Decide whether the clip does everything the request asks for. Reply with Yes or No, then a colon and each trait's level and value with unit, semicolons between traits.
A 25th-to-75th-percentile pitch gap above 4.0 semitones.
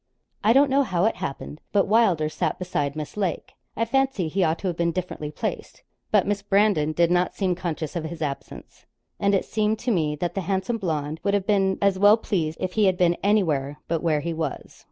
Yes: average, 4.4 semitones